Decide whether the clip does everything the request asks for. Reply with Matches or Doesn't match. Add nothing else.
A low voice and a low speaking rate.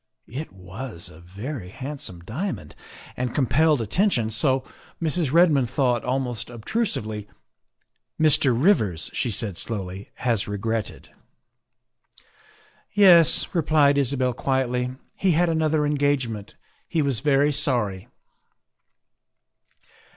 Matches